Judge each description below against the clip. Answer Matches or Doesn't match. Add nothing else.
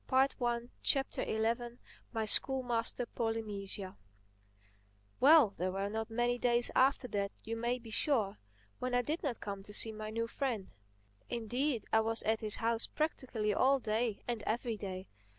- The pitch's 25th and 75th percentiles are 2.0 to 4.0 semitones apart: Matches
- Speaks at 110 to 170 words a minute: Matches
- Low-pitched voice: Doesn't match